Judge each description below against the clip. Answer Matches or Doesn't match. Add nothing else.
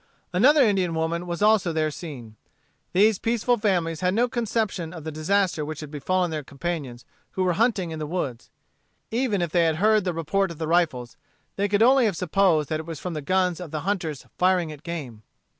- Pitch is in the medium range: Matches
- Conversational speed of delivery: Doesn't match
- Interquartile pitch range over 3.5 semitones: Matches